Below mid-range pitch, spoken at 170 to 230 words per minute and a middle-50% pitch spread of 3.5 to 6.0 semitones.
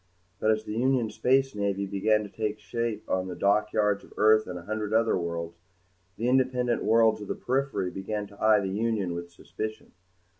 No: low, 105 Hz; average, 190 wpm; narrow, 2.5 semitones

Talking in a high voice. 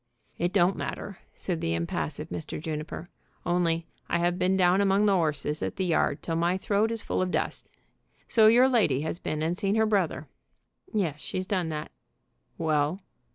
No: medium, 175 Hz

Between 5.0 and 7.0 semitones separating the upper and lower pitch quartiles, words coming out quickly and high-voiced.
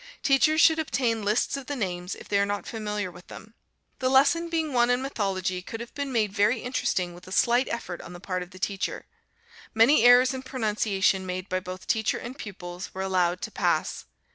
Yes: wide, 5.5 semitones; fast, 210 wpm; high, 215 Hz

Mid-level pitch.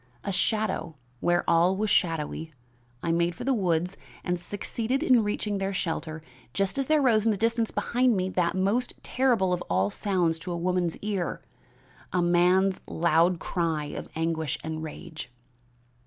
Yes: medium, 180 Hz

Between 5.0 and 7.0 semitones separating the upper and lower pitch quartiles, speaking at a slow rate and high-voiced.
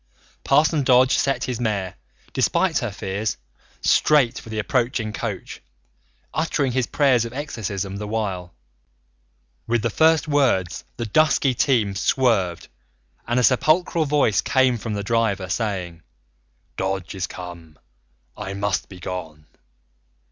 No: average, 5.3 semitones; slow, 130 wpm; low, 115 Hz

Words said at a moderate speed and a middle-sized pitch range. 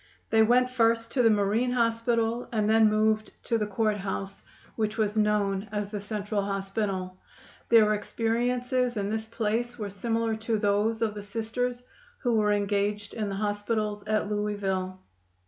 No: average, 160 wpm; narrow, 1.8 semitones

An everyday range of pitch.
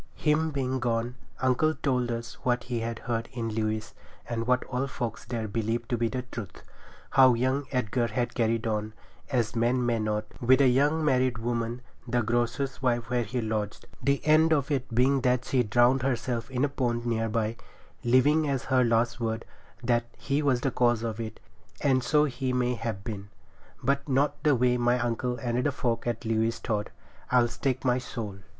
No: narrow, 2.2 semitones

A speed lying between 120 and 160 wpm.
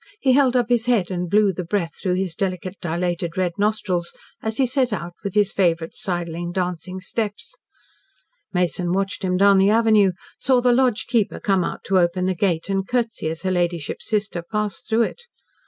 No: average, 190 wpm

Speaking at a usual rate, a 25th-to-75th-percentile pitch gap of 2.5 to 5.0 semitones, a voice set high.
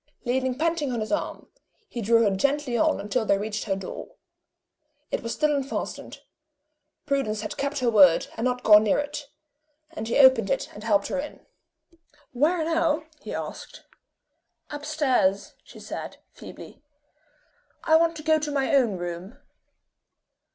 No: average, 160 wpm; wide, 5.6 semitones; very high, 255 Hz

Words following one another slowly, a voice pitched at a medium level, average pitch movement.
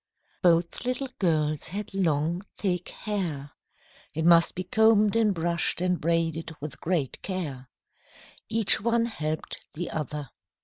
Yes: slow, 130 wpm; medium, 170 Hz; average, 4.4 semitones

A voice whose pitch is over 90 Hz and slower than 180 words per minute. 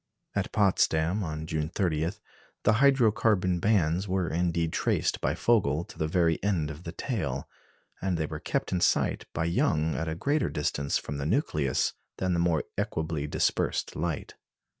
No: very low, 85 Hz; average, 170 wpm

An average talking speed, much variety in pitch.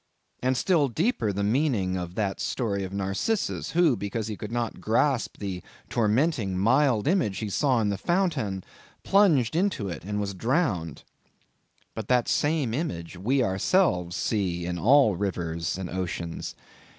Yes: average, 150 wpm; wide, 6.4 semitones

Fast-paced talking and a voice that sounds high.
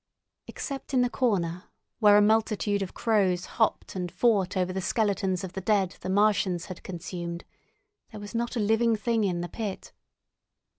No: average, 170 wpm; high, 200 Hz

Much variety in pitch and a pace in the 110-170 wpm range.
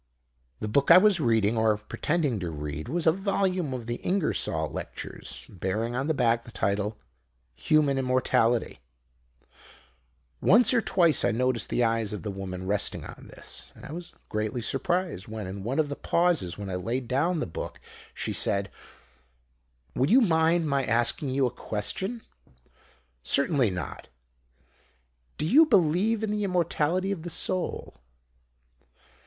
Yes: wide, 8.3 semitones; average, 155 wpm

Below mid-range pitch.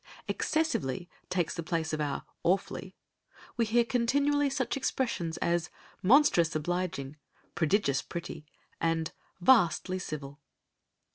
No: medium, 175 Hz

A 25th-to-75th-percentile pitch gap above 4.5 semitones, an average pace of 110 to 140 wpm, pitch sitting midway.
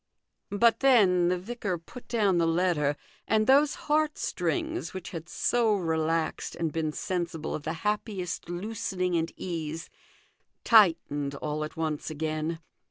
Yes: average, 5.1 semitones; slow, 135 wpm; medium, 175 Hz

